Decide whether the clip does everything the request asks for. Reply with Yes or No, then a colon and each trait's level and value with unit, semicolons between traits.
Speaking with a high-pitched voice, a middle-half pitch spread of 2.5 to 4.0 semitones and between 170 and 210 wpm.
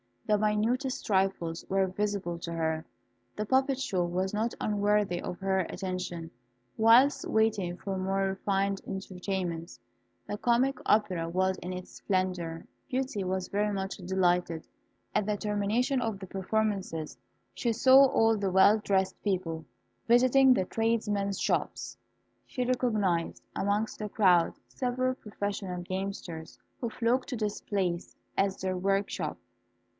No: high, 195 Hz; average, 3.0 semitones; slow, 135 wpm